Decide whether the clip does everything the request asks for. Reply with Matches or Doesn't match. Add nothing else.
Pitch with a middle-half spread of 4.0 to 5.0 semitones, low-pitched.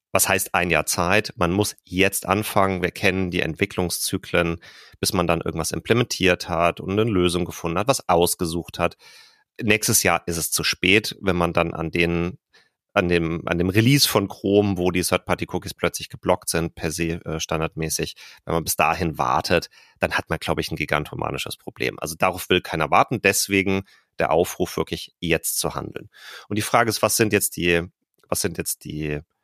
Doesn't match